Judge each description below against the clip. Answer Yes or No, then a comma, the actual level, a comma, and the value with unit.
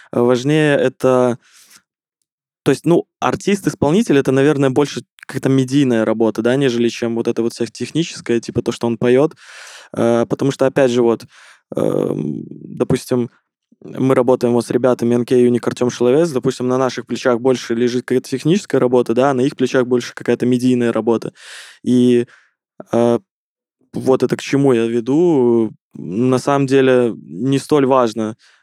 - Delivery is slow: No, average, 150 wpm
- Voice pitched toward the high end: No, low, 125 Hz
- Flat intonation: Yes, narrow, 1.9 semitones